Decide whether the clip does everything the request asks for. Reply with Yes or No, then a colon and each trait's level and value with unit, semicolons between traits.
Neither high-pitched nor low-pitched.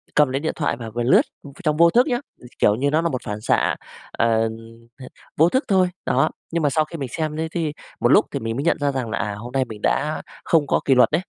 Yes: medium, 145 Hz